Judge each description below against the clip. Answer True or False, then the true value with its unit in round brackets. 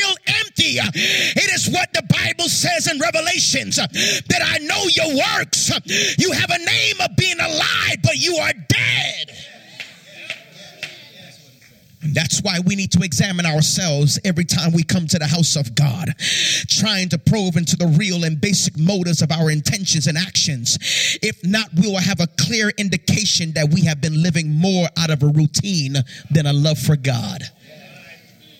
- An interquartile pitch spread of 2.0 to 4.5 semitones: True (3.4 semitones)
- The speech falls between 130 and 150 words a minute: False (165 wpm)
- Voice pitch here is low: False (165 Hz)